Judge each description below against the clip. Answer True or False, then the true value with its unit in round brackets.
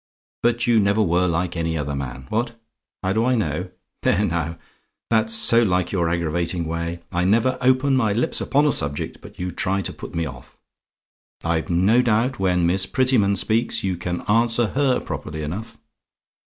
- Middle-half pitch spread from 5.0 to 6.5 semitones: True (5.5 semitones)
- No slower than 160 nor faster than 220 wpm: True (180 wpm)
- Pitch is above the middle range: False (95 Hz)